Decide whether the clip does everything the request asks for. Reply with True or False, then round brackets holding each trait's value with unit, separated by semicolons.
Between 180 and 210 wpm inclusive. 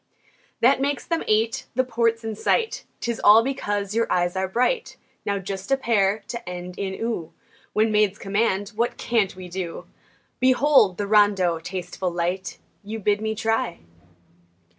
False (160 wpm)